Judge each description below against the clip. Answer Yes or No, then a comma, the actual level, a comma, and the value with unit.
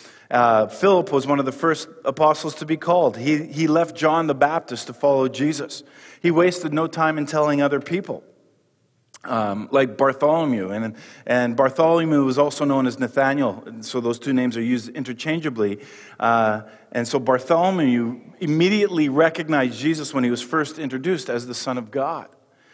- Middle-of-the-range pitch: Yes, medium, 145 Hz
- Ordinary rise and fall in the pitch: Yes, average, 4.3 semitones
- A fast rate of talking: No, average, 170 wpm